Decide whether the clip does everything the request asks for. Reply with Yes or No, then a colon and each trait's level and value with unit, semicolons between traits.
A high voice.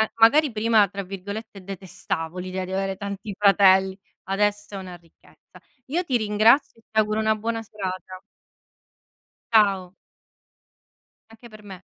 Yes: high, 200 Hz